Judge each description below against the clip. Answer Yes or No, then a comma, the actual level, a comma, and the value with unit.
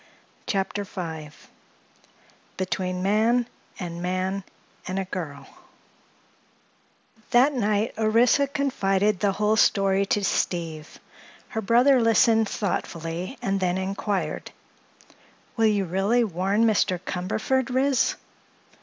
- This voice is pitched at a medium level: No, high, 200 Hz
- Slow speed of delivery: Yes, slow, 100 wpm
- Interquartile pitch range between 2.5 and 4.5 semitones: Yes, average, 3.6 semitones